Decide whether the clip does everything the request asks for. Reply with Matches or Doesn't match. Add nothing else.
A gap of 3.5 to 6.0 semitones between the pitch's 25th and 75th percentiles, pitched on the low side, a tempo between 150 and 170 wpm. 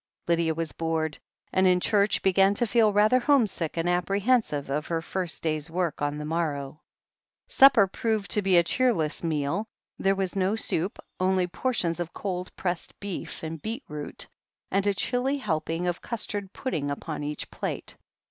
Doesn't match